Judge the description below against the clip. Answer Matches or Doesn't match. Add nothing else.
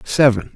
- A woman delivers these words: Doesn't match